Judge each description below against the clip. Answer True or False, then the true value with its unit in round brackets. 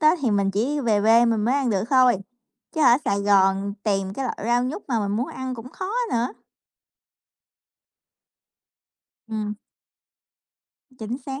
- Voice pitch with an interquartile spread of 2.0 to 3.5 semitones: False (4.1 semitones)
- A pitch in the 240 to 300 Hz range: False (230 Hz)